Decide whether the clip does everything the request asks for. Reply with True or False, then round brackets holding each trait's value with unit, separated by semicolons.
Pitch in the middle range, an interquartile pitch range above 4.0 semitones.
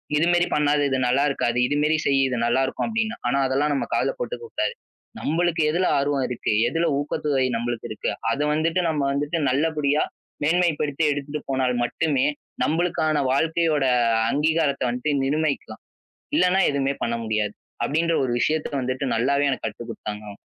False (145 Hz; 3.4 semitones)